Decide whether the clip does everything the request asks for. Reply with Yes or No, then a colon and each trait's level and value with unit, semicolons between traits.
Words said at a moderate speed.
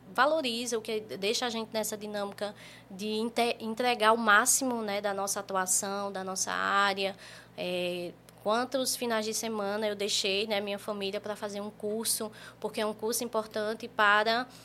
Yes: average, 160 wpm